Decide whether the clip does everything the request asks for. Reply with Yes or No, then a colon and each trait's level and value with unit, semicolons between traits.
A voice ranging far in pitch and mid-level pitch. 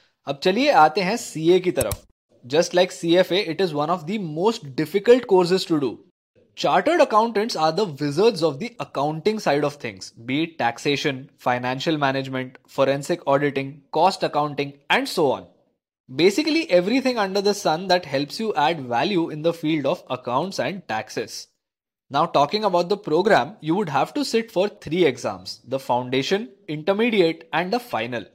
Yes: wide, 6.2 semitones; medium, 175 Hz